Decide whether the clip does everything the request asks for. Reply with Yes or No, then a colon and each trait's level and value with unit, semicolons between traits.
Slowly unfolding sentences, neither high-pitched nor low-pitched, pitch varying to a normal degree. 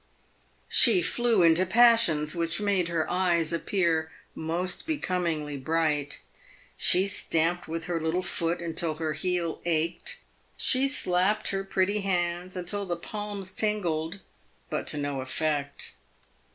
Yes: slow, 125 wpm; medium, 175 Hz; average, 3.3 semitones